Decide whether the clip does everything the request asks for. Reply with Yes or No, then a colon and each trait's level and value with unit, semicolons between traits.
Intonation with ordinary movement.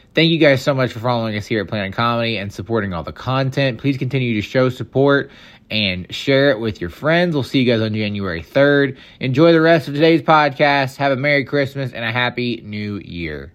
Yes: average, 4.4 semitones